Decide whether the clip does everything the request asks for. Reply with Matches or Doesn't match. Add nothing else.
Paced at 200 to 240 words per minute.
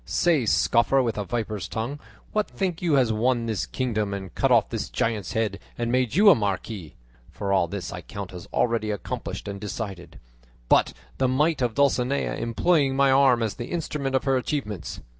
Doesn't match